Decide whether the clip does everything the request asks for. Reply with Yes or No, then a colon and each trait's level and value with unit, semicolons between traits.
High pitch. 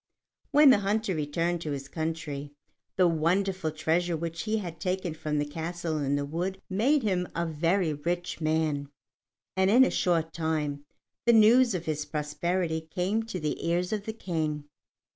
No: medium, 170 Hz